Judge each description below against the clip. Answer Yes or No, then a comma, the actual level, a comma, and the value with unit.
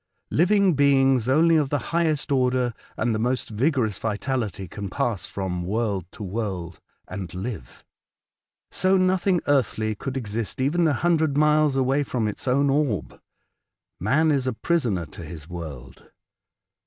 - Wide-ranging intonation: Yes, wide, 6.3 semitones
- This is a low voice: Yes, low, 125 Hz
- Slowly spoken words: No, average, 150 wpm